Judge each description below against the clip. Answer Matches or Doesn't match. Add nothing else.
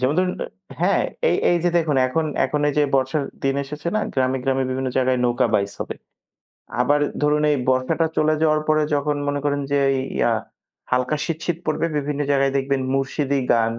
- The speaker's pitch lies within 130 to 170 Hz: Matches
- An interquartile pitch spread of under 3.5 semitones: Matches